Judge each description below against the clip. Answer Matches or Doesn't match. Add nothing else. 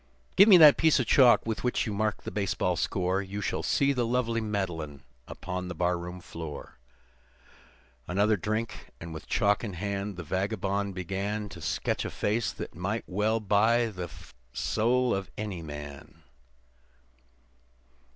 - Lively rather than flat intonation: Doesn't match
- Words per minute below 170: Matches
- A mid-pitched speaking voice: Doesn't match